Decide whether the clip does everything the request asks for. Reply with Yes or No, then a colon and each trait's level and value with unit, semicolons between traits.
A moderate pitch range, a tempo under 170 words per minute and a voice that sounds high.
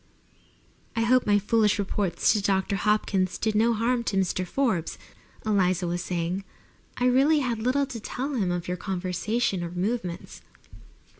Yes: average, 4.5 semitones; average, 155 wpm; high, 205 Hz